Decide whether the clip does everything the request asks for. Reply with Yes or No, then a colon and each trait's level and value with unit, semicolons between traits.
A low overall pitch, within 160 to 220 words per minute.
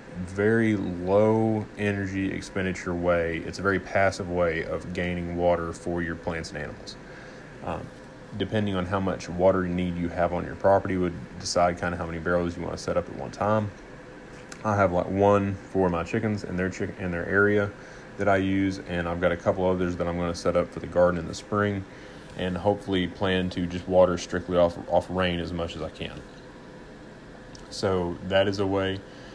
Yes: very low, 90 Hz; average, 200 wpm